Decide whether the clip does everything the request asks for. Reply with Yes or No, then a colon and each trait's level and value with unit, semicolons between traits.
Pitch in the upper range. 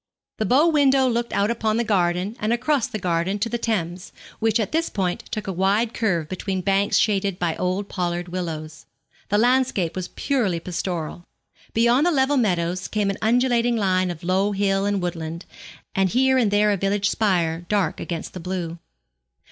Yes: high, 200 Hz